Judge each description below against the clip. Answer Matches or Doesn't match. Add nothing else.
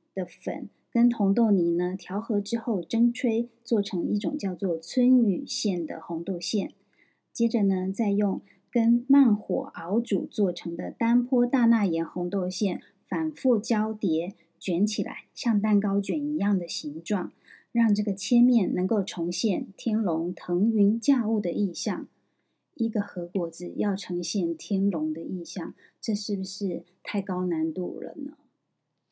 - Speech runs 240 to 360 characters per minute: Doesn't match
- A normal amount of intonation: Matches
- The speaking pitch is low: Doesn't match